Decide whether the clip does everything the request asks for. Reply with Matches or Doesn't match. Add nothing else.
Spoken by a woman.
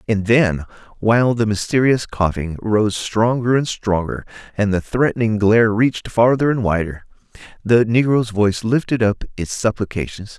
Doesn't match